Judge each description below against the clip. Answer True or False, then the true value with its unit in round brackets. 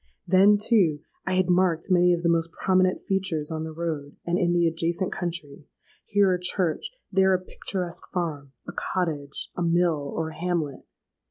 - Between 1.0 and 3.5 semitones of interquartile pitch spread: True (2.5 semitones)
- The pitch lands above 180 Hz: False (175 Hz)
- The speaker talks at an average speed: True (150 wpm)